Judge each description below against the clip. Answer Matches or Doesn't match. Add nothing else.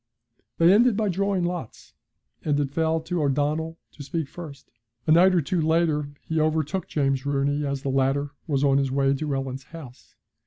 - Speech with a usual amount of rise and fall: Matches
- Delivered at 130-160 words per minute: Doesn't match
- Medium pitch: Matches